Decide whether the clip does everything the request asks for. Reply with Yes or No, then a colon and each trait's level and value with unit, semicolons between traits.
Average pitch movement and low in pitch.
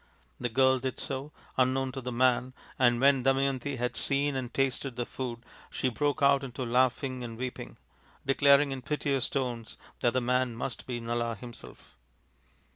No: narrow, 1.9 semitones; low, 130 Hz